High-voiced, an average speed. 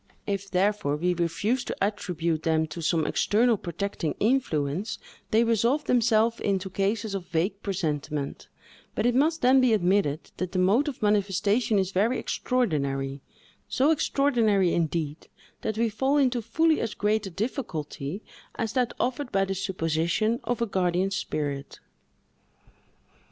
Yes: high, 200 Hz; average, 145 wpm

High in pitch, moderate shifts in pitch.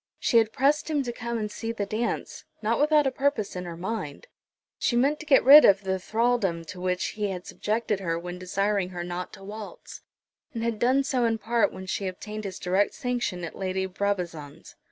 Yes: high, 210 Hz; average, 4.4 semitones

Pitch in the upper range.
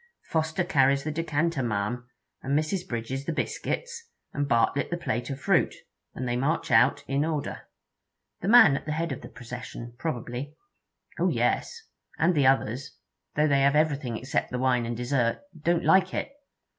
No: medium, 140 Hz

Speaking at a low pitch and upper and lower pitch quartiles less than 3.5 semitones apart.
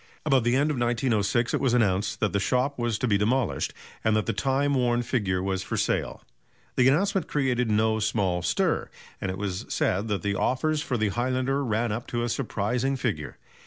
No: low, 120 Hz; average, 4.0 semitones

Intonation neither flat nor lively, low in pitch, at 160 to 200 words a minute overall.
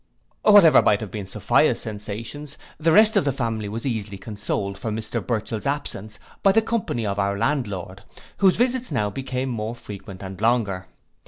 No: wide, 5.7 semitones; low, 110 Hz; average, 170 wpm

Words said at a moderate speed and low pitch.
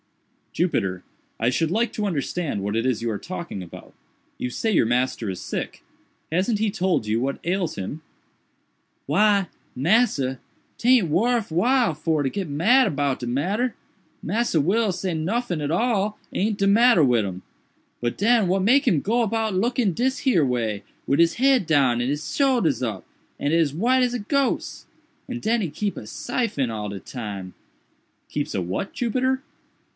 No: average, 170 wpm; medium, 175 Hz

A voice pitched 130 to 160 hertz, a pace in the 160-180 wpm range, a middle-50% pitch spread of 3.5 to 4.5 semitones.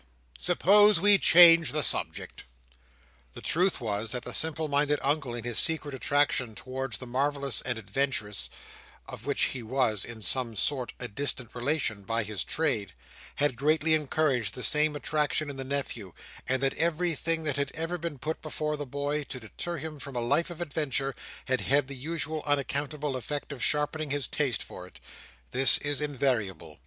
Yes: medium, 140 Hz; average, 170 wpm; average, 3.8 semitones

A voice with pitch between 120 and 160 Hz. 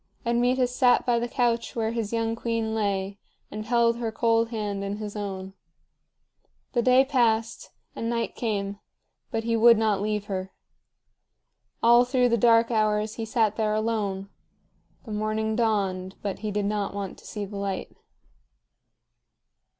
No: high, 220 Hz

